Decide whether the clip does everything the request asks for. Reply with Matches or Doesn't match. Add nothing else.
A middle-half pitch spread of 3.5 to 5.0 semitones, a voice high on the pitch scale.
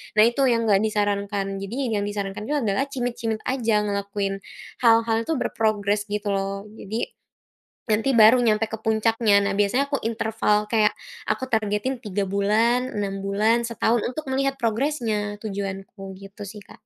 Doesn't match